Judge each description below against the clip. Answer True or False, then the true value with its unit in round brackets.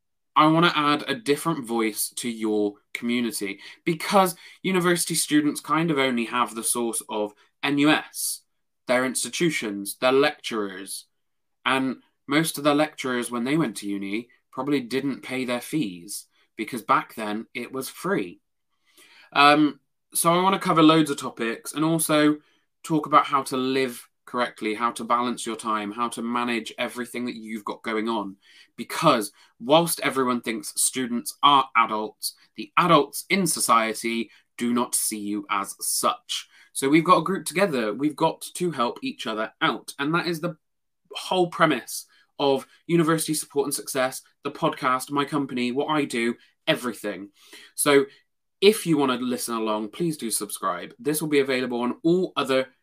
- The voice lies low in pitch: True (130 Hz)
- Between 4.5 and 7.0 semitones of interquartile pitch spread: True (5.0 semitones)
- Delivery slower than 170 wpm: True (160 wpm)